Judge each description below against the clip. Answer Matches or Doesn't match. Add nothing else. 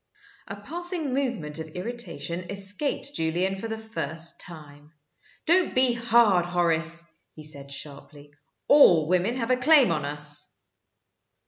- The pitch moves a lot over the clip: Matches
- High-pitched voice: Doesn't match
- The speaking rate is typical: Doesn't match